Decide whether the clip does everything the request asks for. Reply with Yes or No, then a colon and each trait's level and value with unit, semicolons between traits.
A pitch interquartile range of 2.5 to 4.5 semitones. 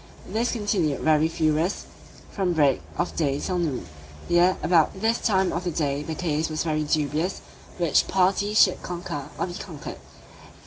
Yes: average, 3.5 semitones